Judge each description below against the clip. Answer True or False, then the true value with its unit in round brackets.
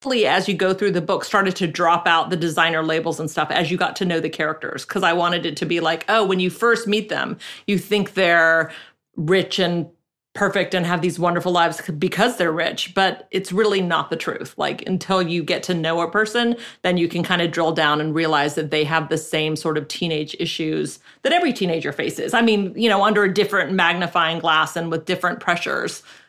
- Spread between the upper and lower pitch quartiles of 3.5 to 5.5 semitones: False (2.8 semitones)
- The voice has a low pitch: False (175 Hz)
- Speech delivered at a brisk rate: True (225 wpm)